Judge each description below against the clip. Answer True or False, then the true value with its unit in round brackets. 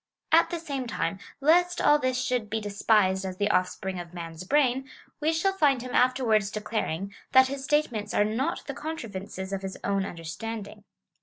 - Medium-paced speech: True (180 wpm)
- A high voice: True (225 Hz)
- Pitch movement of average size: False (5.9 semitones)